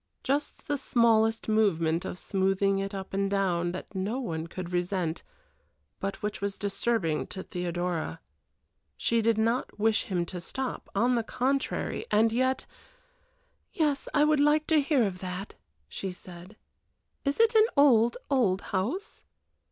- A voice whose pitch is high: Yes, high, 205 Hz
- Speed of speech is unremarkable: Yes, average, 150 wpm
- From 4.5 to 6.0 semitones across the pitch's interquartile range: Yes, wide, 5.5 semitones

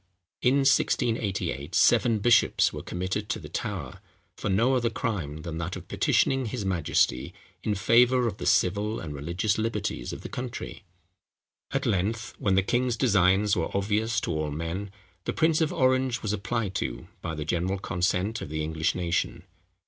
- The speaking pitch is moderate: No, low, 100 Hz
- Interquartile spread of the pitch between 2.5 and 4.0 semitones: No, average, 5.2 semitones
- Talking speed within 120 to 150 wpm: No, average, 170 wpm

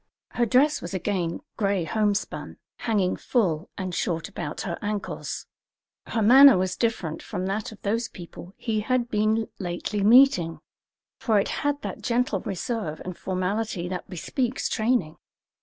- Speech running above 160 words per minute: No, average, 145 wpm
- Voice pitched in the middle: No, high, 205 Hz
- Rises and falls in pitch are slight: No, average, 4.2 semitones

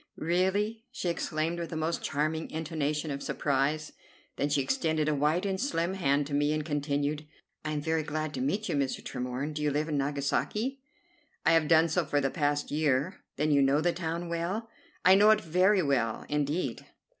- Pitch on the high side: No, medium, 155 Hz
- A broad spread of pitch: No, average, 3.0 semitones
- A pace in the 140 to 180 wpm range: No, average, 195 wpm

